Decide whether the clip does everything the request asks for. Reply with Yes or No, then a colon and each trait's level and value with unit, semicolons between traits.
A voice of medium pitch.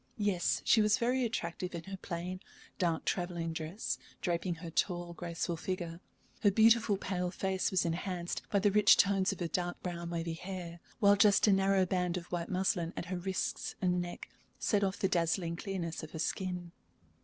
Yes: medium, 180 Hz